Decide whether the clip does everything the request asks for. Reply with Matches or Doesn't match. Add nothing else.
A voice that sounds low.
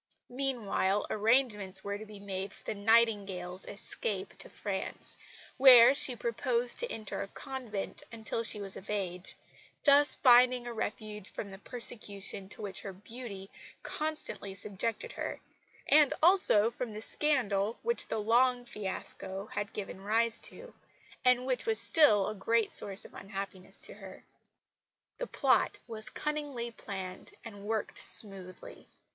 Doesn't match